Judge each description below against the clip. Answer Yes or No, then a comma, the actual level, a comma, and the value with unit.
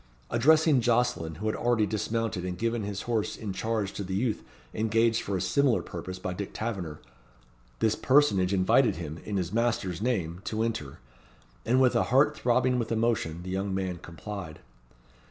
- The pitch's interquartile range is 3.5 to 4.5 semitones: Yes, average, 4.1 semitones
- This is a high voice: No, low, 105 Hz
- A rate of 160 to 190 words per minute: Yes, average, 170 wpm